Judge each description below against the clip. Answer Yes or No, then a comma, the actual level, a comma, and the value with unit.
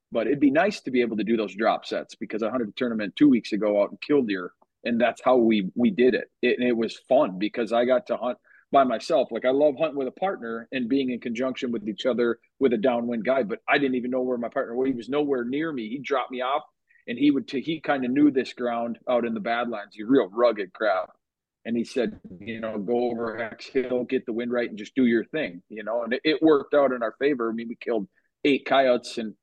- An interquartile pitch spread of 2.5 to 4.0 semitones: Yes, average, 2.8 semitones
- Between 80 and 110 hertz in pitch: No, low, 120 Hz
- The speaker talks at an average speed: No, fast, 270 wpm